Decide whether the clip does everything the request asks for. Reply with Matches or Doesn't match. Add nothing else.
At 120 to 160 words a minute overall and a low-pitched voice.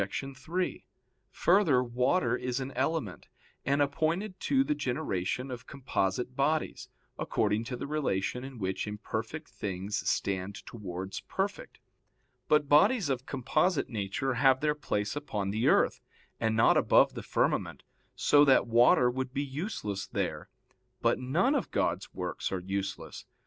Matches